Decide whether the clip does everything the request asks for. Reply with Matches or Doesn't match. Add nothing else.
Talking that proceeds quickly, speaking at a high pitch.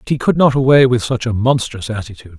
Doesn't match